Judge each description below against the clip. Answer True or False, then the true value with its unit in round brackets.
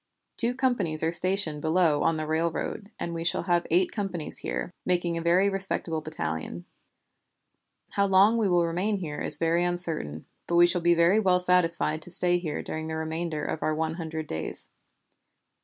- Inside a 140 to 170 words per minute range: False (180 wpm)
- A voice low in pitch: False (170 Hz)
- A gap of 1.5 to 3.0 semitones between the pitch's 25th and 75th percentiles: True (2.4 semitones)